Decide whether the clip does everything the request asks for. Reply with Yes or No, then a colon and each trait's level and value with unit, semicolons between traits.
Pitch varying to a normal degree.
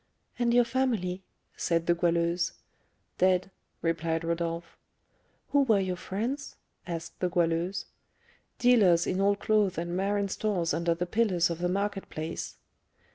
Yes: average, 3.2 semitones